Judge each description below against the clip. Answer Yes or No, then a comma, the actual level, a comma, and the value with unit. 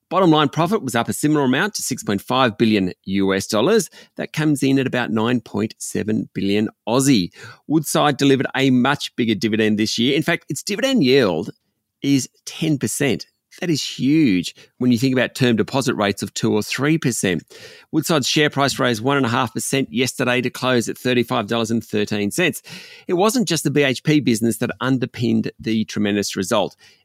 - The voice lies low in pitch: Yes, low, 125 Hz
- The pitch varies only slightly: No, average, 4.4 semitones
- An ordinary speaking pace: Yes, average, 160 wpm